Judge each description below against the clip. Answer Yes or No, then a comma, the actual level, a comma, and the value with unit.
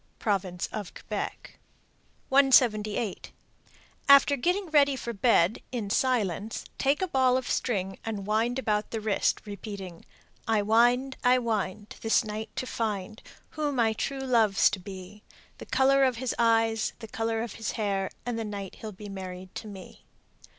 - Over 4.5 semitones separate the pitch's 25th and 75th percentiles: No, average, 3.8 semitones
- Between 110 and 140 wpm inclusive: No, average, 155 wpm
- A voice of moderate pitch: No, high, 225 Hz